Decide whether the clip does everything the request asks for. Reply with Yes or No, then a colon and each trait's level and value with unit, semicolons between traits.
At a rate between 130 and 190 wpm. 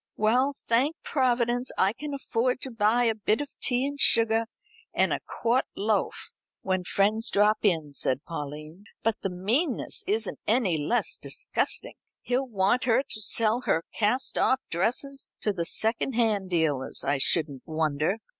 Yes: average, 155 wpm